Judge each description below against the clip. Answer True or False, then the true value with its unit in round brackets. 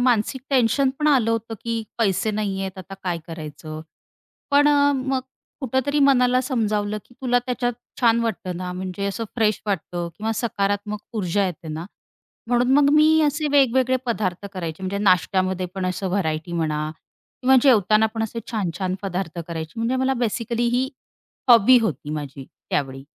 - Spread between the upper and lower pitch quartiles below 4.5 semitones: False (5.4 semitones)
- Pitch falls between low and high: False (215 Hz)